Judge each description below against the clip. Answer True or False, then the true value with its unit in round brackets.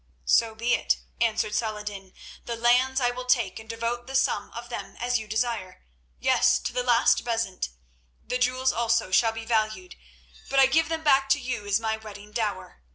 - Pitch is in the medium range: False (230 Hz)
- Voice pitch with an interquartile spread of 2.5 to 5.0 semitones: True (2.8 semitones)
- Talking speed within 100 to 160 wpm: False (185 wpm)